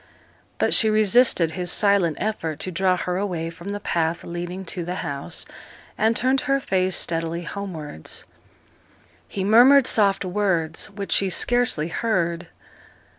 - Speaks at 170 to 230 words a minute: No, average, 140 wpm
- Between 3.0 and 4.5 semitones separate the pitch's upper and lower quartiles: Yes, average, 3.6 semitones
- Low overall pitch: No, medium, 185 Hz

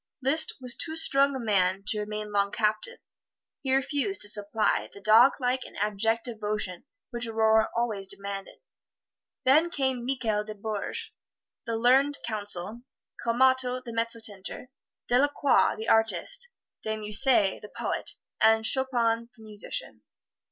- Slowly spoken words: Yes, slow, 130 wpm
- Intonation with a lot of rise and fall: No, average, 3.7 semitones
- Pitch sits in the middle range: No, high, 225 Hz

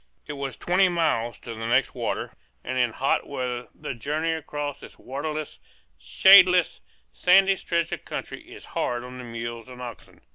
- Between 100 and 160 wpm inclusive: No, average, 170 wpm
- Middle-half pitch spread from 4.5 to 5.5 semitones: Yes, average, 5.1 semitones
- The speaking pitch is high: No, low, 135 Hz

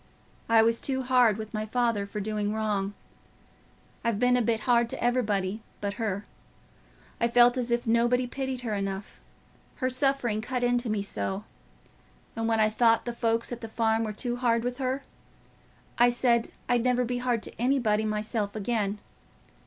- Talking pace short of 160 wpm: No, average, 170 wpm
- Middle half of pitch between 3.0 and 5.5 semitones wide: No, narrow, 2.4 semitones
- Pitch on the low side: No, high, 230 Hz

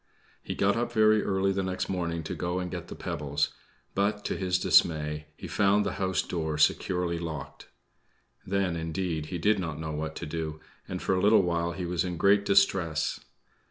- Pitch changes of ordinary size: Yes, average, 3.4 semitones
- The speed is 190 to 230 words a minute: Yes, average, 195 wpm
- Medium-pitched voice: No, very low, 90 Hz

